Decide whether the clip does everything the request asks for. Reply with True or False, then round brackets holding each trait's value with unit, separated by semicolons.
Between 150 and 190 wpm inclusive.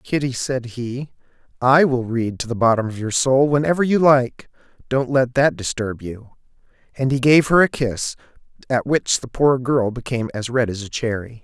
False (200 wpm)